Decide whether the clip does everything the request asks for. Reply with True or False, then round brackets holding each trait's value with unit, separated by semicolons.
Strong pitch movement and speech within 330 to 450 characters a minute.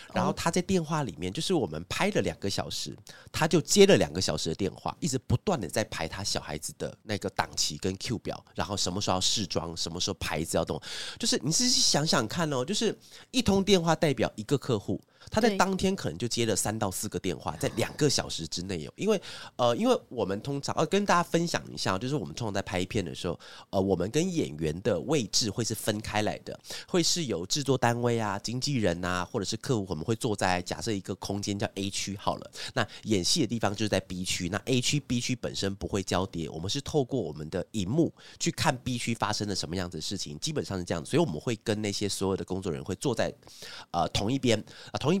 True (6.8 semitones; 350 characters per minute)